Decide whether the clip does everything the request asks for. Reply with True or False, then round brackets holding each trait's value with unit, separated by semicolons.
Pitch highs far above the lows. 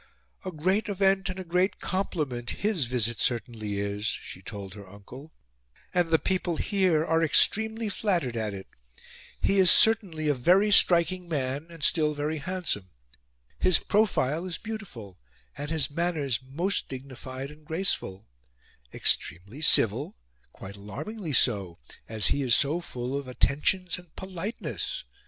True (7.3 semitones)